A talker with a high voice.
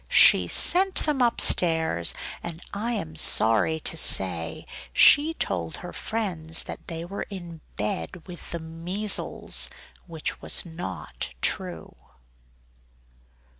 No: medium, 165 Hz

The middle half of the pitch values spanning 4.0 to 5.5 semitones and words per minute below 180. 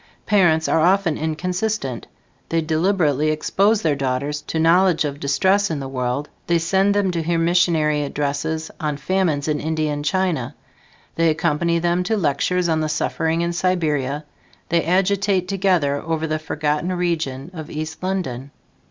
No: average, 3.4 semitones; average, 160 wpm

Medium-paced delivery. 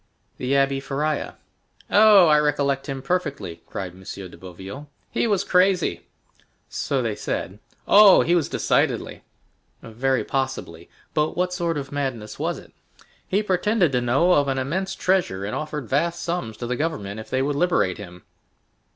Yes: average, 160 wpm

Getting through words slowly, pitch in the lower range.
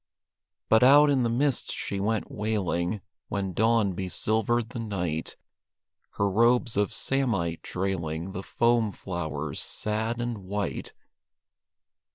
Yes: slow, 120 wpm; low, 105 Hz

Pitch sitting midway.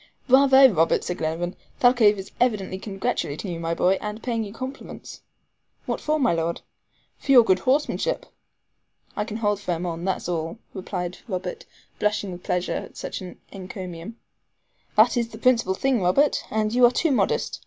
No: high, 205 Hz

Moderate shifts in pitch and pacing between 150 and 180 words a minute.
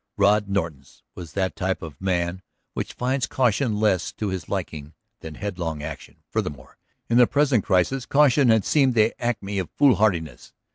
No: wide, 5.8 semitones; average, 160 wpm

